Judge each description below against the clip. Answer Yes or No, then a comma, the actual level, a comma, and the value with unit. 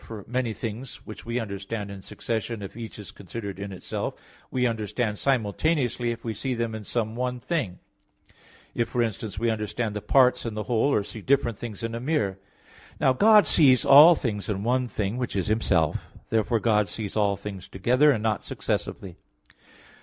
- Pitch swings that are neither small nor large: Yes, average, 3.2 semitones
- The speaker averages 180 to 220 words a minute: Yes, average, 185 wpm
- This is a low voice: Yes, low, 115 Hz